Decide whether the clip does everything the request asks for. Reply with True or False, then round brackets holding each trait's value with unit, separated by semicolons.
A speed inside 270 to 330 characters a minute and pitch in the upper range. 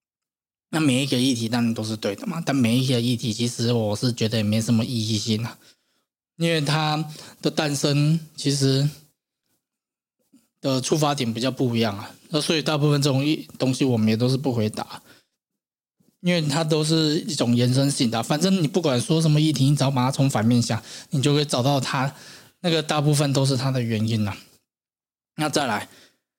False (275 characters per minute; 135 Hz)